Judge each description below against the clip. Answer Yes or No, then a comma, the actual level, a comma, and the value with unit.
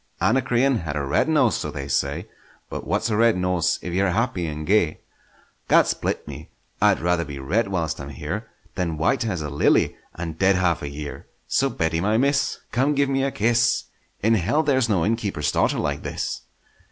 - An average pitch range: No, wide, 6.7 semitones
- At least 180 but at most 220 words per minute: Yes, average, 190 wpm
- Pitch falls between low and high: No, very low, 90 Hz